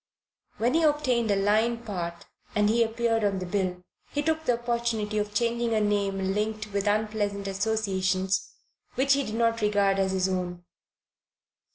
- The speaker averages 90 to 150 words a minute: No, average, 165 wpm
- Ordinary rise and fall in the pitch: Yes, average, 3.0 semitones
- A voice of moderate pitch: No, high, 210 Hz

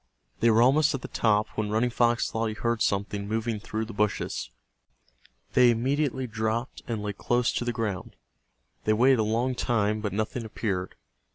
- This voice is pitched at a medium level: No, low, 115 Hz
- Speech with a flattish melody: Yes, narrow, 2.2 semitones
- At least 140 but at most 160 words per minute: No, average, 180 wpm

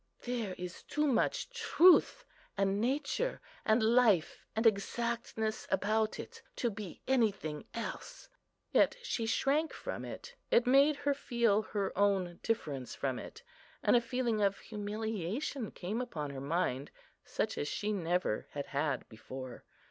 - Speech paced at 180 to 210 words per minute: No, average, 140 wpm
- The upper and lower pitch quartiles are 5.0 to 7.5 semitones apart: Yes, wide, 5.6 semitones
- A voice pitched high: Yes, high, 220 Hz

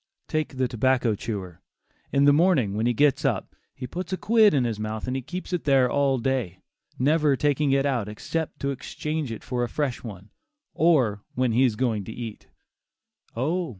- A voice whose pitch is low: Yes, low, 130 Hz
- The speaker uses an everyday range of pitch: Yes, average, 4.5 semitones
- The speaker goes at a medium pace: Yes, average, 190 wpm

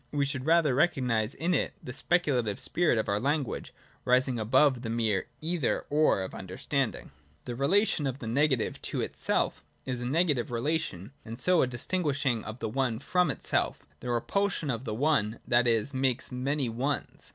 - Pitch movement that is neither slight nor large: Yes, average, 4.4 semitones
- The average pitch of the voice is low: Yes, low, 130 Hz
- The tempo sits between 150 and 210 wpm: Yes, average, 195 wpm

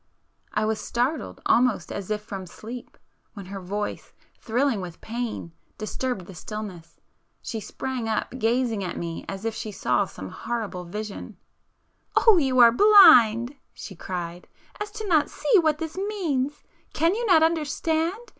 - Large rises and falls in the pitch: Yes, wide, 7.0 semitones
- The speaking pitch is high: Yes, high, 230 Hz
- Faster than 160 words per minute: No, average, 155 wpm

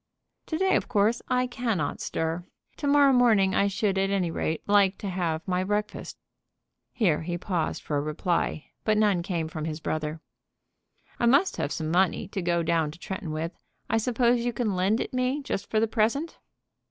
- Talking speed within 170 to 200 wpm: Yes, average, 190 wpm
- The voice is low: No, high, 195 Hz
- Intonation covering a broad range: Yes, wide, 5.8 semitones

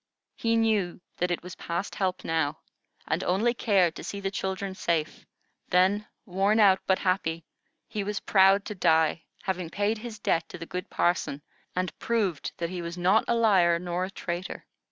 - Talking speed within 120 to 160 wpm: No, average, 180 wpm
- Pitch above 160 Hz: Yes, medium, 185 Hz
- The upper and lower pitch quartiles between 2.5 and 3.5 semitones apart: Yes, average, 2.9 semitones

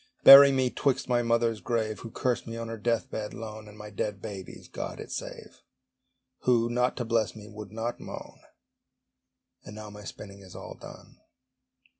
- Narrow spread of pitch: Yes, narrow, 2.1 semitones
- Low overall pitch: Yes, low, 115 Hz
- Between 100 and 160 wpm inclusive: No, average, 180 wpm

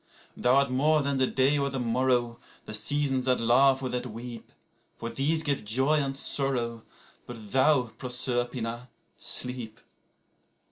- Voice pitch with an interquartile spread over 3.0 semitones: No, narrow, 2.4 semitones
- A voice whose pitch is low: Yes, low, 130 Hz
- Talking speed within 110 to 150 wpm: Yes, average, 140 wpm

